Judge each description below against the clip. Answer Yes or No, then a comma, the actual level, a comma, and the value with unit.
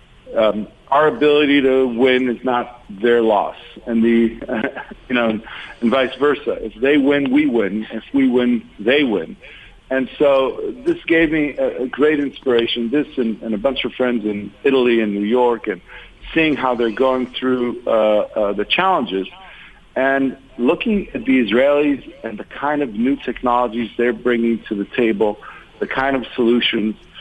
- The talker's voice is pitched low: Yes, low, 125 Hz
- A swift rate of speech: No, average, 170 wpm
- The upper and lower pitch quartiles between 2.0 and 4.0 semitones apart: Yes, average, 3.3 semitones